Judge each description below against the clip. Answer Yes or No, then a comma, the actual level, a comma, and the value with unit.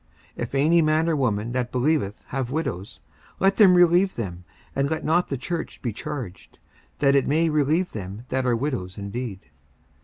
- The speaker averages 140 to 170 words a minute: No, average, 180 wpm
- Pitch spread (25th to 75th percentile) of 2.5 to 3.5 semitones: No, wide, 5.5 semitones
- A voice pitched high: No, low, 135 Hz